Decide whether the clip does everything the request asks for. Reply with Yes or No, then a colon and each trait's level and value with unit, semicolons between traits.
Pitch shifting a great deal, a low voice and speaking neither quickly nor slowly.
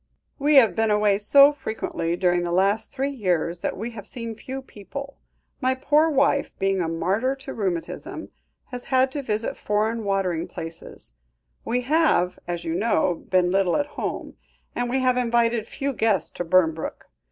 No: wide, 6.3 semitones; high, 220 Hz; average, 170 wpm